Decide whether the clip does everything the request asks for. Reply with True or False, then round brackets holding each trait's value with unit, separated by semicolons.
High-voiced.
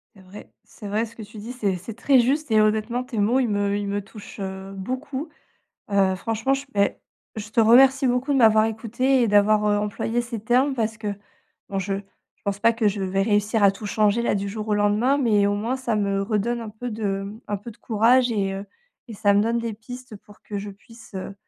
True (215 Hz)